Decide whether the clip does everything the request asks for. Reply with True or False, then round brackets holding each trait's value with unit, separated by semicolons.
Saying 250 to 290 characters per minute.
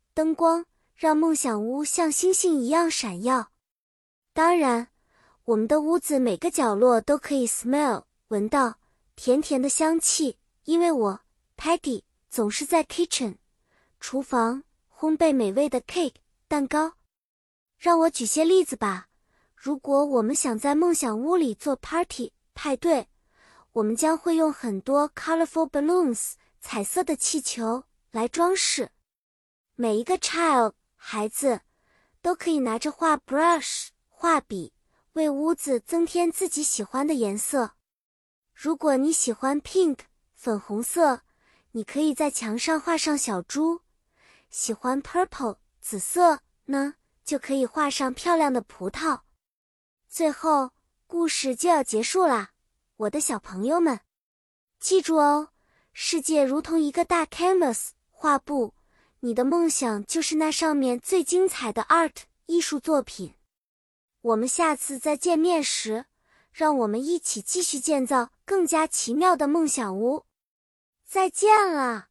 False (235 characters per minute)